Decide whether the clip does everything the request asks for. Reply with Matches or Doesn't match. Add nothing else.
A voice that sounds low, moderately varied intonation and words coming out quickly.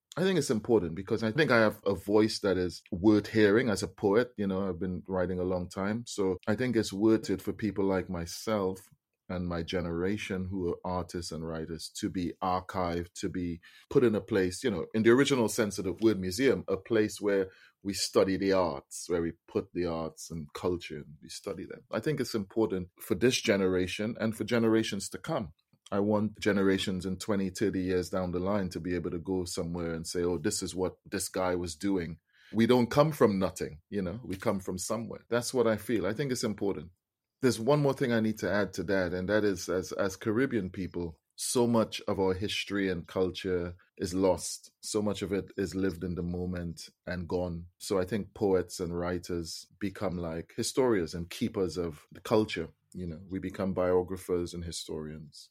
Matches